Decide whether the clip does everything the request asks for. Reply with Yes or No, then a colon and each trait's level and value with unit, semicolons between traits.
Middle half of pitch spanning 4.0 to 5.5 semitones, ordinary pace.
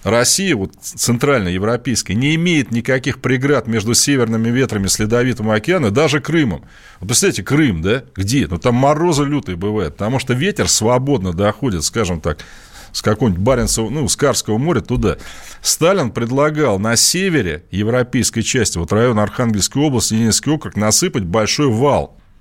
Yes: average, 4.9 semitones; average, 150 wpm